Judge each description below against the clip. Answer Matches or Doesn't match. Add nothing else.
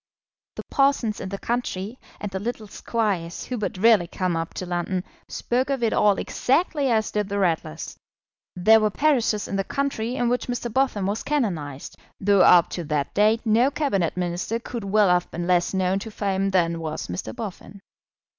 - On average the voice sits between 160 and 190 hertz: Doesn't match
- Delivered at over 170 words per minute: Matches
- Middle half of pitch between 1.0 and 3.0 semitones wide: Doesn't match